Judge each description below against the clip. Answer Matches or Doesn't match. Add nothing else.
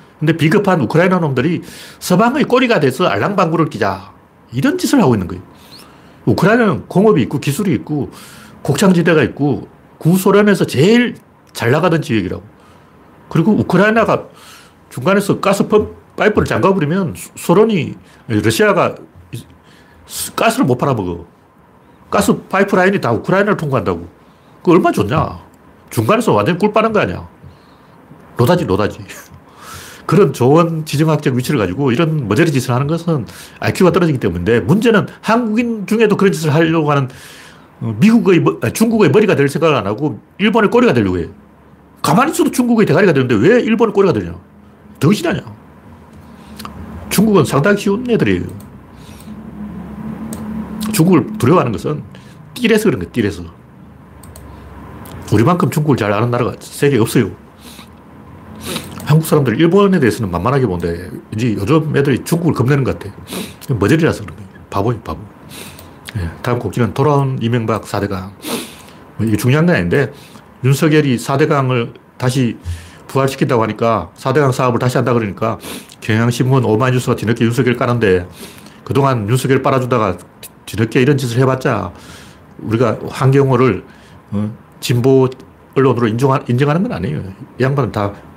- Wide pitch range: Matches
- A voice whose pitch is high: Doesn't match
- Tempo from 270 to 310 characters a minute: Doesn't match